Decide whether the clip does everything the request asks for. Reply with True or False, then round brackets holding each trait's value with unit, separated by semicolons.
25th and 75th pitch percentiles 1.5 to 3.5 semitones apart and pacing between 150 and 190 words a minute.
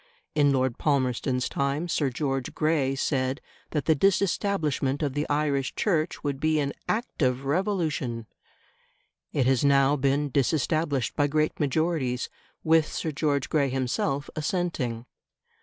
False (2.8 semitones; 135 wpm)